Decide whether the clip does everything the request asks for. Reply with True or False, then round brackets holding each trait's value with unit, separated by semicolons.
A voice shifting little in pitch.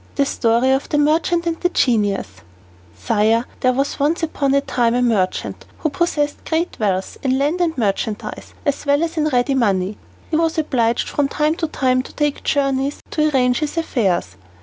False (4.8 semitones)